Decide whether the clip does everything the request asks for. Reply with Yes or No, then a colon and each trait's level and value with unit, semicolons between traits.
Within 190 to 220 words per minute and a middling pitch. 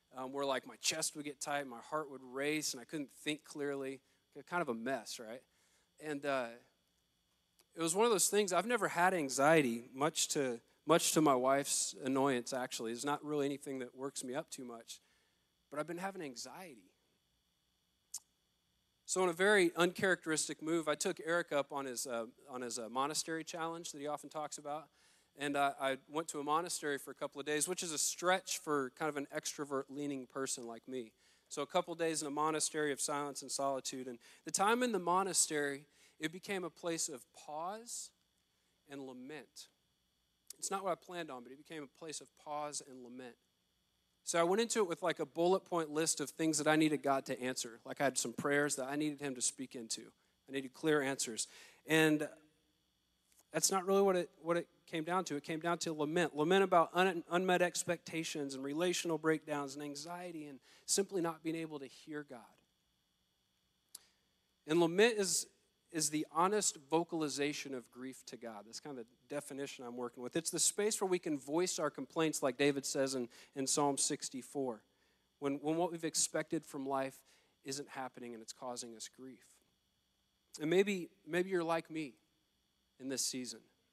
Yes: average, 195 wpm; medium, 150 Hz